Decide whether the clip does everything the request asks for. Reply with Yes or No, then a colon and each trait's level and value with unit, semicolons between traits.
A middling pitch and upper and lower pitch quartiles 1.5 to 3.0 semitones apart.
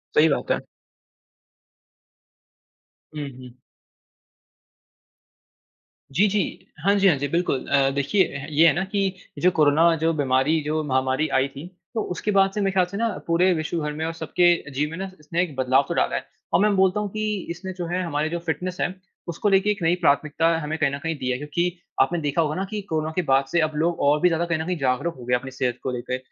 No: medium, 160 Hz; average, 4.2 semitones